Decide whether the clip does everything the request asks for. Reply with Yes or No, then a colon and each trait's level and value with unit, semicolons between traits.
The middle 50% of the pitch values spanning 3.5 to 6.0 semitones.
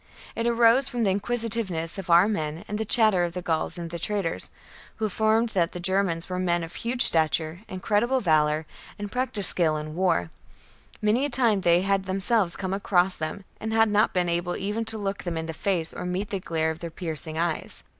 Yes: average, 4.3 semitones